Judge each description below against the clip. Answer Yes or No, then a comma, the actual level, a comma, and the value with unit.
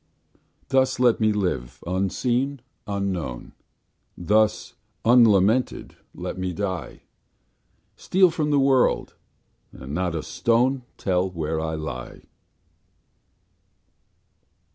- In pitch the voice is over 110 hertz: No, low, 100 Hz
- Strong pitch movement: Yes, wide, 6.4 semitones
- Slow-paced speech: Yes, slow, 95 wpm